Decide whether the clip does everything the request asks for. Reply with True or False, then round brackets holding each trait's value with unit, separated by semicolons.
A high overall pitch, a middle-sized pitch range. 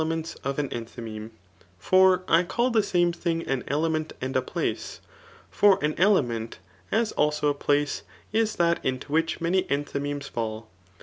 False (150 Hz; 4.4 semitones)